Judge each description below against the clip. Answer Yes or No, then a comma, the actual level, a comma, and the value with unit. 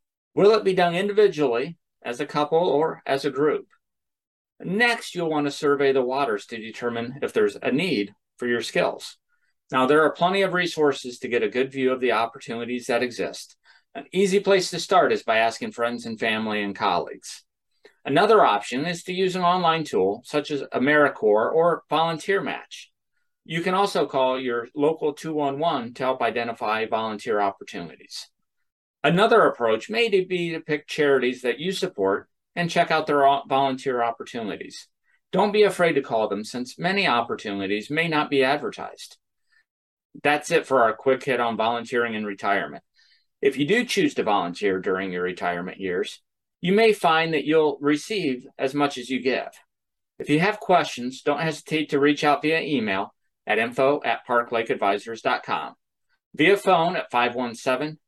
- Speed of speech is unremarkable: Yes, average, 170 wpm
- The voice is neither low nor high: Yes, medium, 145 Hz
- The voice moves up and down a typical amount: No, wide, 6.3 semitones